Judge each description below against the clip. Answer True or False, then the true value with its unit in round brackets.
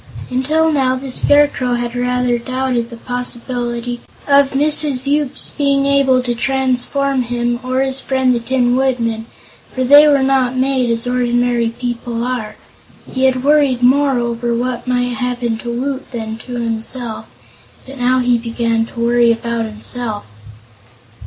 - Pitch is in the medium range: False (250 Hz)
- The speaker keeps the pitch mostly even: True (1.9 semitones)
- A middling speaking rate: True (150 wpm)